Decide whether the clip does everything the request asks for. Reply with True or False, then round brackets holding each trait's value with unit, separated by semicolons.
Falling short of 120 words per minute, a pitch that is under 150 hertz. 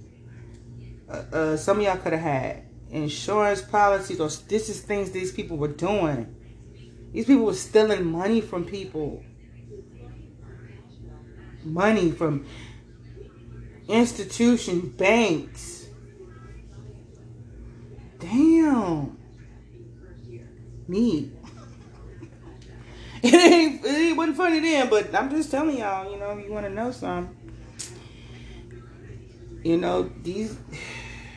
True (100 wpm; 140 Hz)